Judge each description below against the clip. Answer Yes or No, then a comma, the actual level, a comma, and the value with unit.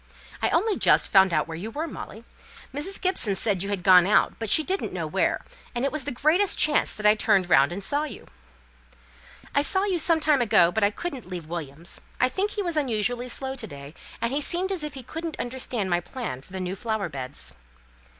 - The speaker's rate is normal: No, fast, 225 wpm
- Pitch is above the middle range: Yes, high, 235 Hz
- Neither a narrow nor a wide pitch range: No, wide, 8.4 semitones